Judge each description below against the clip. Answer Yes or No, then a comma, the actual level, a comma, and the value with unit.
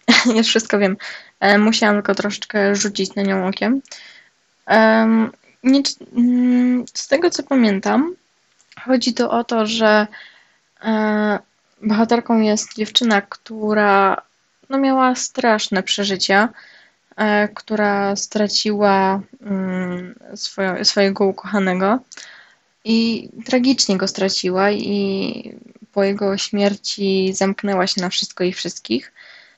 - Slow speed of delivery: Yes, slow, 95 wpm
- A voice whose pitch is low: No, high, 210 Hz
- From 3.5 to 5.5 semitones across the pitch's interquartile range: No, average, 2.7 semitones